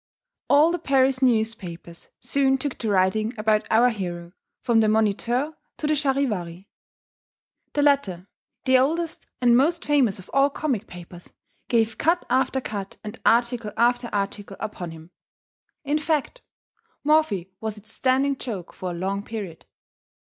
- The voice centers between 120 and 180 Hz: No, high, 230 Hz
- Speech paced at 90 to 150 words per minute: Yes, average, 145 wpm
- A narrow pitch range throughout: No, wide, 5.6 semitones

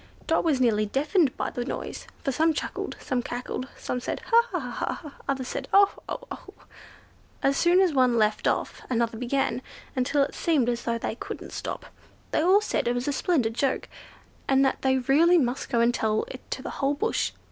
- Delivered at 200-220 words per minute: Yes, fast, 205 wpm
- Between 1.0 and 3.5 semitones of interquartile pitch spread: No, average, 4.2 semitones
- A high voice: Yes, very high, 265 Hz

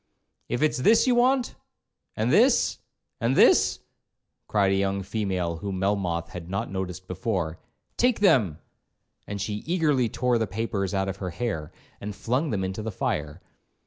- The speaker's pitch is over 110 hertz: No, low, 100 Hz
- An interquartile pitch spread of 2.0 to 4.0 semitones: No, average, 4.7 semitones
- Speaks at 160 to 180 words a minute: No, average, 150 wpm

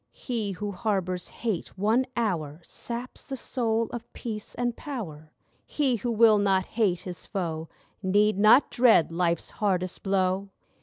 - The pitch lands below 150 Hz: No, high, 205 Hz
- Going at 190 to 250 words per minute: No, average, 145 wpm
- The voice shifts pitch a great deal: No, average, 4.2 semitones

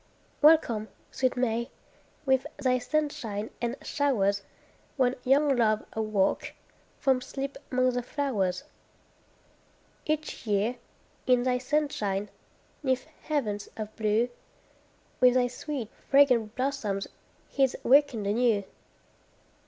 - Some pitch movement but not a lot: Yes, average, 4.2 semitones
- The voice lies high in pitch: Yes, very high, 250 Hz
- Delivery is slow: Yes, slow, 105 wpm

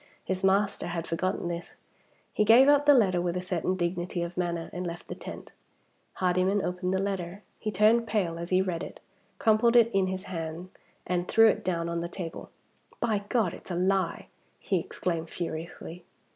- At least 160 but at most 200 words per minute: Yes, average, 190 wpm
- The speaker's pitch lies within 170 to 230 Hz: Yes, medium, 185 Hz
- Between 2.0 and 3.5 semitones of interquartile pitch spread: Yes, average, 2.7 semitones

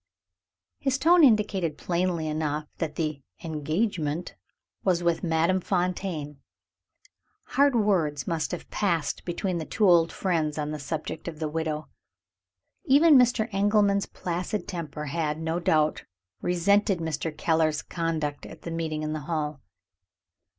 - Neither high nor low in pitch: Yes, medium, 165 Hz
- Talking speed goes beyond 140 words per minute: No, slow, 135 wpm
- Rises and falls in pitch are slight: No, average, 3.8 semitones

